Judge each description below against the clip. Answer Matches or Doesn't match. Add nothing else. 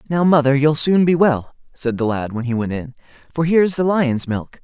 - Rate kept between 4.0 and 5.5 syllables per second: Matches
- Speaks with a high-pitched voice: Doesn't match